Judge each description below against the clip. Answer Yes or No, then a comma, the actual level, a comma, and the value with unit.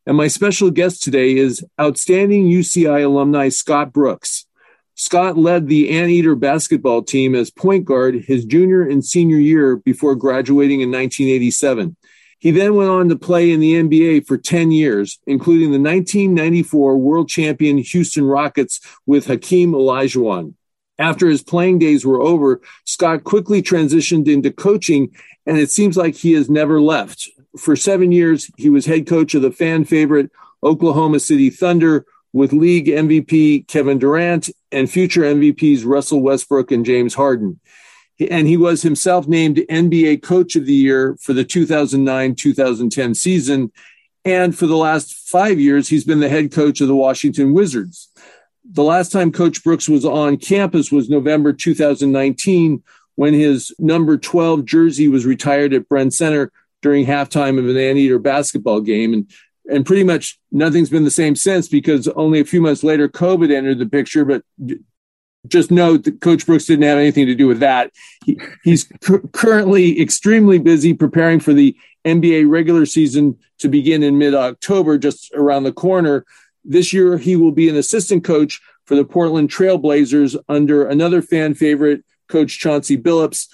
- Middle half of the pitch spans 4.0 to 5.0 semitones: No, average, 3.2 semitones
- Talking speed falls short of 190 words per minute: Yes, average, 160 wpm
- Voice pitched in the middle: Yes, medium, 155 Hz